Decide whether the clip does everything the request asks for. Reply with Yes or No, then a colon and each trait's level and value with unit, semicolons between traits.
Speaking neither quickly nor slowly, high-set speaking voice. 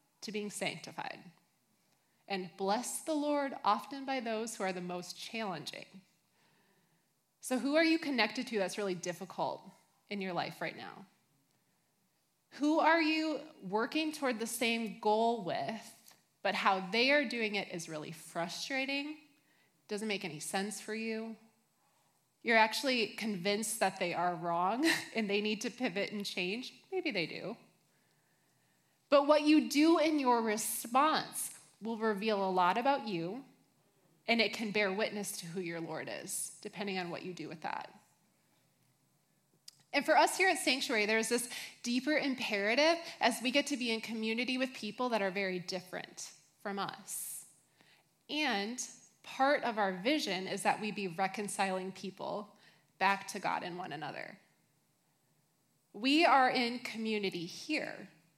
Yes: average, 150 wpm; high, 215 Hz